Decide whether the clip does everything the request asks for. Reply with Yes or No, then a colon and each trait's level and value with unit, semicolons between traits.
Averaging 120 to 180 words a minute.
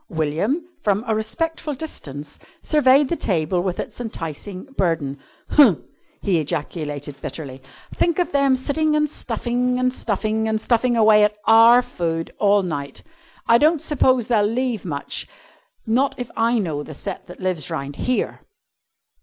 Yes: average, 150 wpm